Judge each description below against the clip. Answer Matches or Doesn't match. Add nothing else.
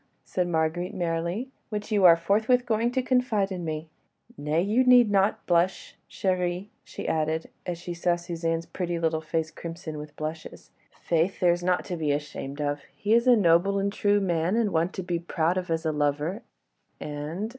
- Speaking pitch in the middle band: Matches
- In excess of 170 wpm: Matches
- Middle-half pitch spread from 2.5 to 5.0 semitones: Matches